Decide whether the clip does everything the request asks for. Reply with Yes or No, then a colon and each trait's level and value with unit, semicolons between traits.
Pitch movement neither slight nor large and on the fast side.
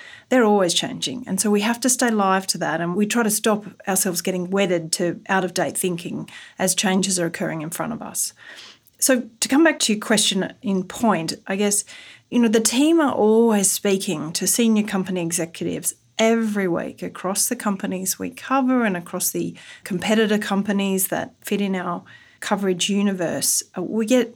No: average, 3.4 semitones; average, 185 wpm